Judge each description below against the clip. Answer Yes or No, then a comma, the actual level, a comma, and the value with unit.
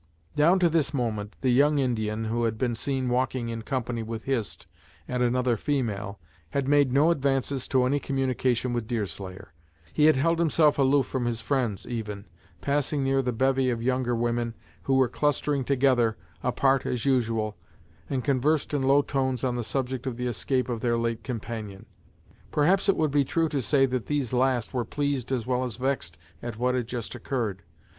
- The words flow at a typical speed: Yes, average, 185 wpm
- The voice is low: Yes, low, 125 Hz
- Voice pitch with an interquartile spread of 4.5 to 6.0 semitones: No, average, 2.9 semitones